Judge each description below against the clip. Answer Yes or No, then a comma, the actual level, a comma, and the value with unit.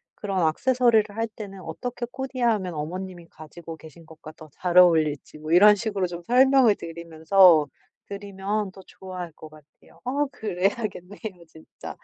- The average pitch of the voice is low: No, medium, 185 Hz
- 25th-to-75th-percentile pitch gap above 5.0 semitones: No, average, 4.6 semitones